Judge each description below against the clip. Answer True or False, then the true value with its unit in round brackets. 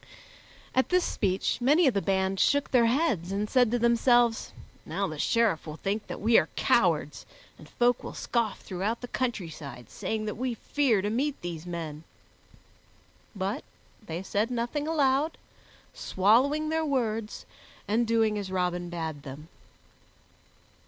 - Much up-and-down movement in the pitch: False (5.0 semitones)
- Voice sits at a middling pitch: False (220 Hz)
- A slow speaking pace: False (150 wpm)